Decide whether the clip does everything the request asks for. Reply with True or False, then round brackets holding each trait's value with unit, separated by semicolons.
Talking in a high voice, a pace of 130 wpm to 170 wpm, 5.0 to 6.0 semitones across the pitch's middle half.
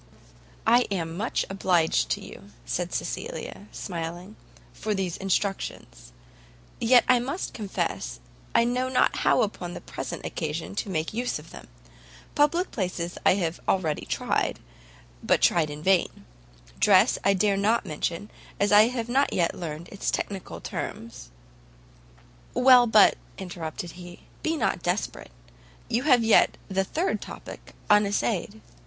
True (195 Hz; 140 wpm; 5.4 semitones)